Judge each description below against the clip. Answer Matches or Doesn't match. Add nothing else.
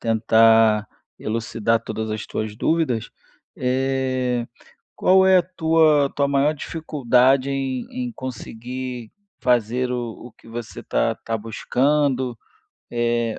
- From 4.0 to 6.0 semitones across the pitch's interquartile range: Doesn't match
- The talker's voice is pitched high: Doesn't match